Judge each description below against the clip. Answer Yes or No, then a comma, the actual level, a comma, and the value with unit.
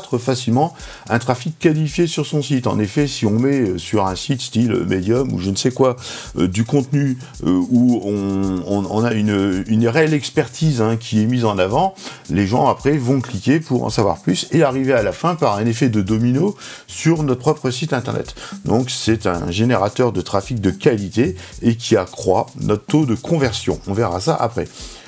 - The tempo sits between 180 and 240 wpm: Yes, average, 200 wpm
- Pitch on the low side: Yes, low, 120 Hz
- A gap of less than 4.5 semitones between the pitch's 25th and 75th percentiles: No, average, 4.8 semitones